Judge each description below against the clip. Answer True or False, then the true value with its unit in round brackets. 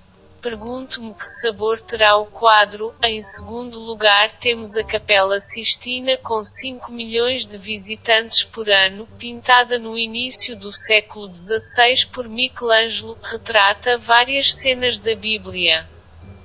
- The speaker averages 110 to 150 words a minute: True (120 wpm)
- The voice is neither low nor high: False (225 Hz)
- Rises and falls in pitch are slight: True (2.3 semitones)